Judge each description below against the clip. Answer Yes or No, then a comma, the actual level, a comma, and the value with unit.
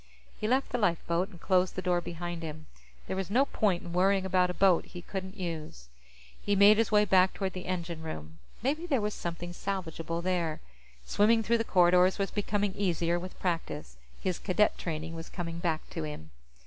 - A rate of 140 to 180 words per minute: No, average, 195 wpm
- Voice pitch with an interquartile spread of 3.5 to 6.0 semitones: No, average, 3.0 semitones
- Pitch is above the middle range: No, medium, 180 Hz